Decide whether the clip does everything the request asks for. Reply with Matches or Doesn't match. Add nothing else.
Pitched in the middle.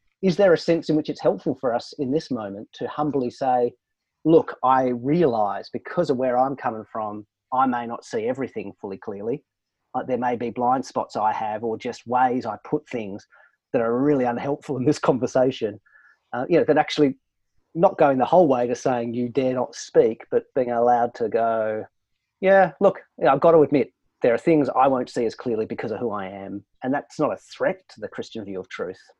Doesn't match